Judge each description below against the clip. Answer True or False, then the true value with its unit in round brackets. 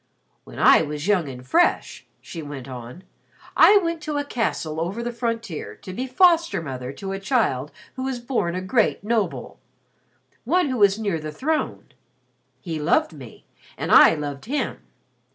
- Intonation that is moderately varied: False (9.0 semitones)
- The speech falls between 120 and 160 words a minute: False (170 wpm)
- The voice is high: True (195 Hz)